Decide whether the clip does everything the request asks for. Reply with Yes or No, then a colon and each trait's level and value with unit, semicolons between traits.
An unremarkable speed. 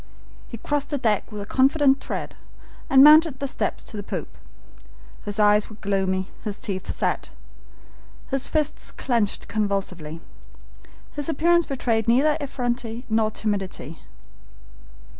No: slow, 130 wpm